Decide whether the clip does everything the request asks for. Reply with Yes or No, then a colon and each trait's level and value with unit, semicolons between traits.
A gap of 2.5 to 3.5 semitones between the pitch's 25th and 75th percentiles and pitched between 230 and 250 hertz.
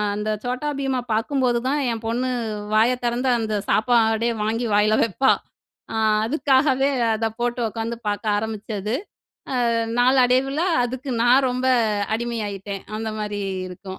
Yes: average, 2.9 semitones; high, 235 Hz